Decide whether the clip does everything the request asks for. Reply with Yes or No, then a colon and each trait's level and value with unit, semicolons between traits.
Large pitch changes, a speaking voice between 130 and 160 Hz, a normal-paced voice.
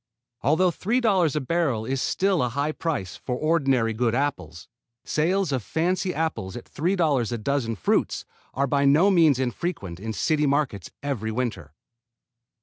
Yes: wide, 5.8 semitones; medium, 140 Hz; average, 155 wpm